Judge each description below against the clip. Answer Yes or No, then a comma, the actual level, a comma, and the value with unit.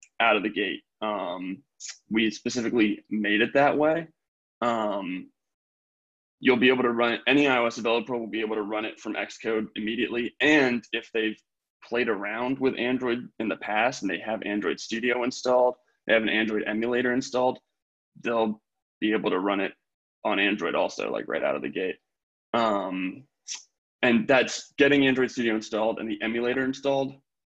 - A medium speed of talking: Yes, average, 170 wpm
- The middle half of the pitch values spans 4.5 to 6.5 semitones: No, average, 2.8 semitones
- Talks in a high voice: No, low, 120 Hz